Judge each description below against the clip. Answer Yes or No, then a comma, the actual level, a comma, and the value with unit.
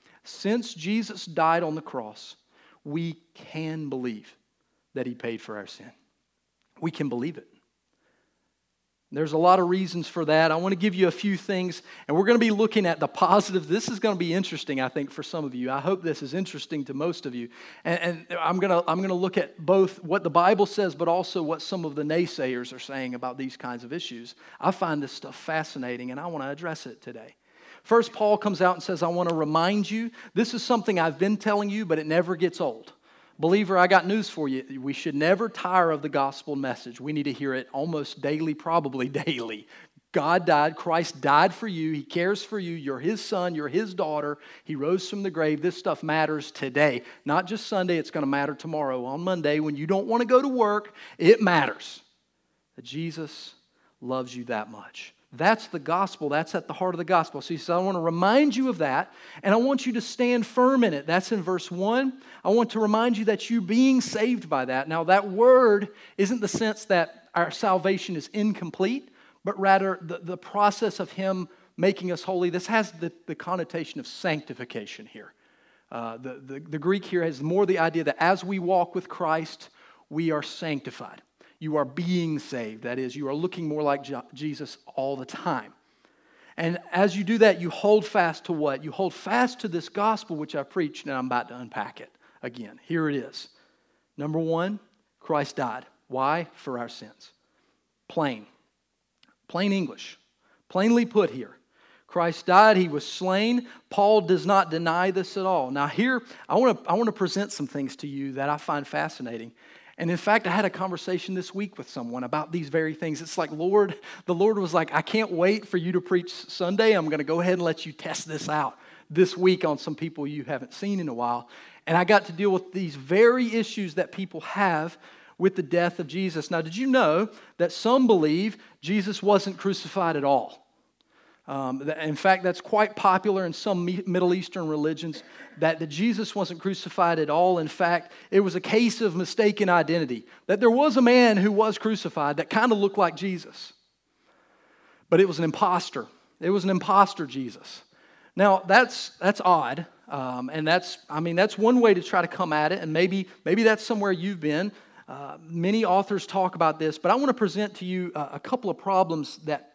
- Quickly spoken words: Yes, fast, 210 wpm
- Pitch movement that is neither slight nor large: Yes, average, 4.5 semitones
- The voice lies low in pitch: No, medium, 175 Hz